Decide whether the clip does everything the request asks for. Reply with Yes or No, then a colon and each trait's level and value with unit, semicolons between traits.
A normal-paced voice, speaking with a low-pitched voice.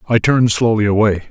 Yes: average, 185 wpm; low, 110 Hz